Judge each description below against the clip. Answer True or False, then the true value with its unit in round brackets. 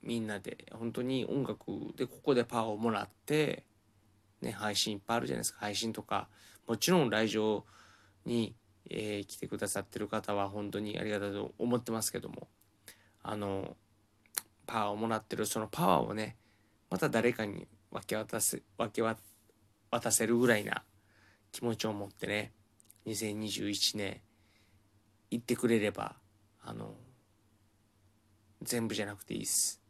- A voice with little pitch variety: True (1.6 semitones)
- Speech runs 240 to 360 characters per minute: True (285 characters per minute)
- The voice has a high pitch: False (105 Hz)